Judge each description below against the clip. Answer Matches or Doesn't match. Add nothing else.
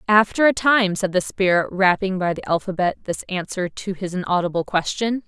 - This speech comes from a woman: Matches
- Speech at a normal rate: Matches